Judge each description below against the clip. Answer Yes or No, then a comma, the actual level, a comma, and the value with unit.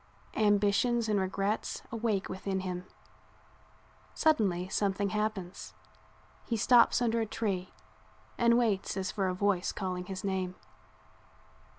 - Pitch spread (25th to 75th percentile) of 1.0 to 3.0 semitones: Yes, average, 2.7 semitones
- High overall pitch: Yes, high, 200 Hz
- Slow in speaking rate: Yes, slow, 115 wpm